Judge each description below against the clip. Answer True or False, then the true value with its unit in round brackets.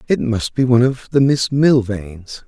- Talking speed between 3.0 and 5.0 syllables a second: True (4.5 syllables/s)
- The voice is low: True (125 Hz)